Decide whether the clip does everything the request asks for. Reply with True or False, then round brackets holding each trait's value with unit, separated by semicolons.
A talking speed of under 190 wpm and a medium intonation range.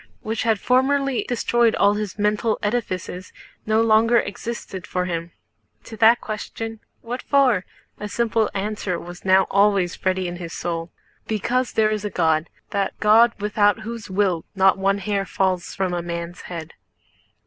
True (160 wpm; 3.5 semitones)